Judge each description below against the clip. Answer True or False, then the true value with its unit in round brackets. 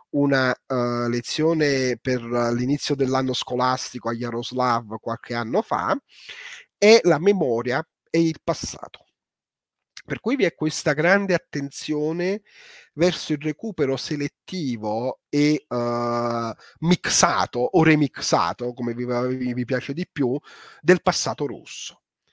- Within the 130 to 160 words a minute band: False (120 wpm)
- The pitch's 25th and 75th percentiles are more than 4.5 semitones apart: True (5.3 semitones)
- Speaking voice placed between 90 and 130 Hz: False (140 Hz)